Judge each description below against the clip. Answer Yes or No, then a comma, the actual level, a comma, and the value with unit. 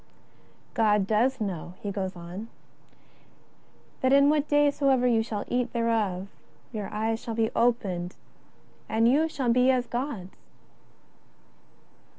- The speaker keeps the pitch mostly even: No, average, 4.0 semitones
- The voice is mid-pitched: No, high, 230 Hz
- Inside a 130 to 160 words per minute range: Yes, average, 140 wpm